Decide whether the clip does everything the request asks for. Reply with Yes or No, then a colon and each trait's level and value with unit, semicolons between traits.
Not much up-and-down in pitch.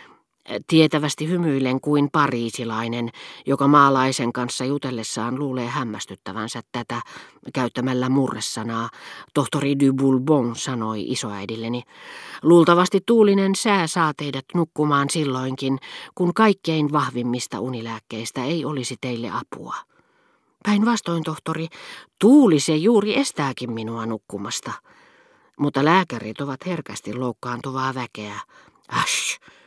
No: average, 4.9 semitones